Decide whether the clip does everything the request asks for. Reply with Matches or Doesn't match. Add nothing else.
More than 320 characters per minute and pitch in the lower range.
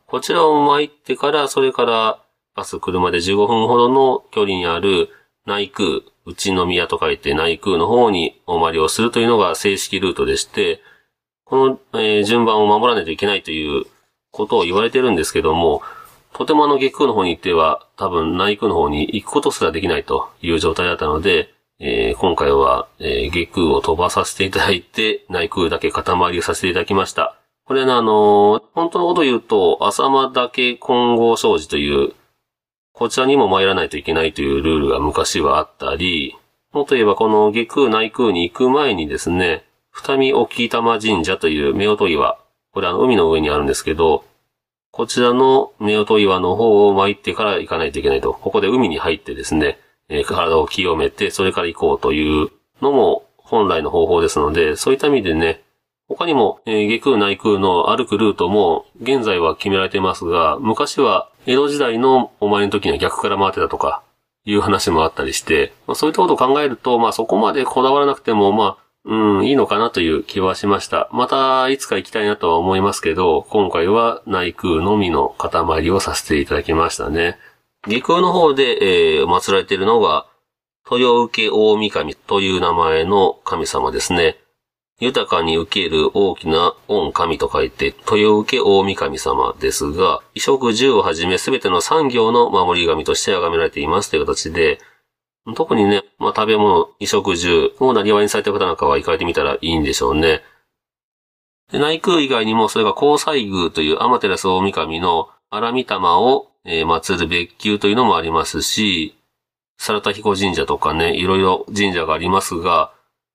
Matches